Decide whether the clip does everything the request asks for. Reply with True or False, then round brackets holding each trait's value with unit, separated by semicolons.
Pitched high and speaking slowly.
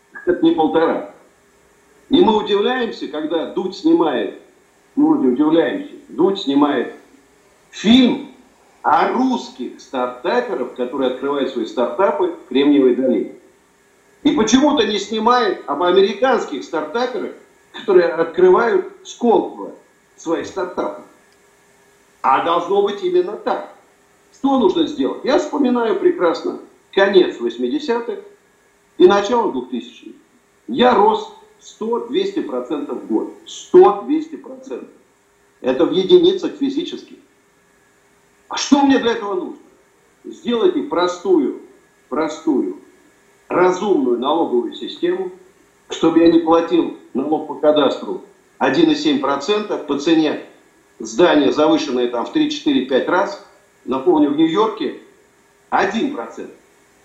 True (300 Hz; 100 wpm)